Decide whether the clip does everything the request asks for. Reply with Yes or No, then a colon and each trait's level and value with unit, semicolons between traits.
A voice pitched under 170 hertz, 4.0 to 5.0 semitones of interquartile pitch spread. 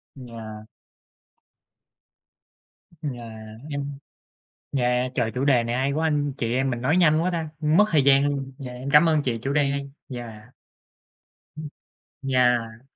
No: low, 135 Hz; average, 3.2 semitones